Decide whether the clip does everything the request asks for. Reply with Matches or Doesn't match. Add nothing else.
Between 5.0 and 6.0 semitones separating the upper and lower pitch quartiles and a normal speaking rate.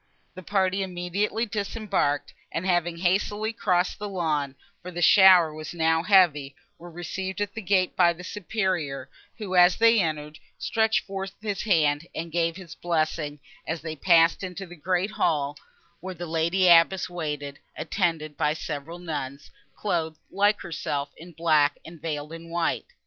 Doesn't match